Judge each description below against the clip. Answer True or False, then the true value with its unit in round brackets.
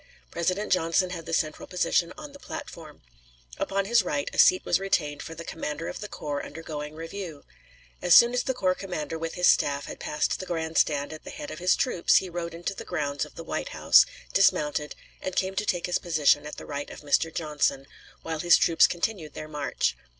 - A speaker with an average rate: False (215 wpm)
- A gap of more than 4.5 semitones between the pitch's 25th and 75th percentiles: False (3.7 semitones)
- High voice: False (165 Hz)